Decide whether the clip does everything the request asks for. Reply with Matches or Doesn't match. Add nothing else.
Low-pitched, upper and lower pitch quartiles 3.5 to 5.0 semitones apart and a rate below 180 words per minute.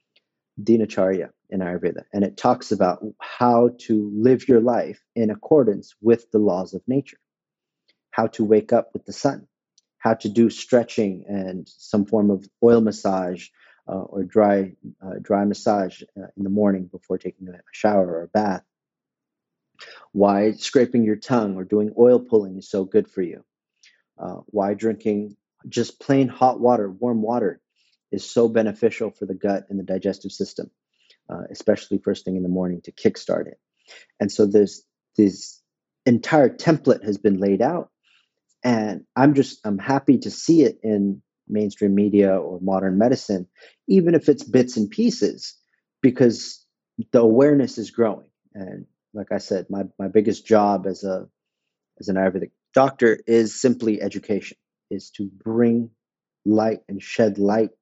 Doesn't match